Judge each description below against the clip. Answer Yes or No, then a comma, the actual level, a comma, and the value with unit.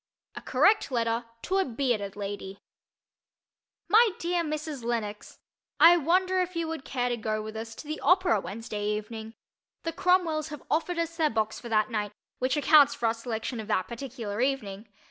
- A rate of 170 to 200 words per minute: Yes, average, 180 wpm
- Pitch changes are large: Yes, wide, 6.9 semitones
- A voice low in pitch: No, high, 245 Hz